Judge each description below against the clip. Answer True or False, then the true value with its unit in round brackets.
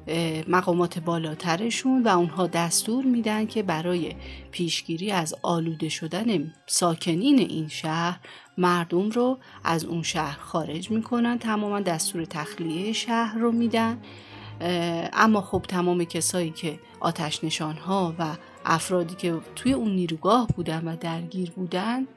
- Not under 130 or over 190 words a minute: False (120 wpm)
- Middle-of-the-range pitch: True (175 Hz)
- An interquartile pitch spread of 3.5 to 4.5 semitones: True (4.2 semitones)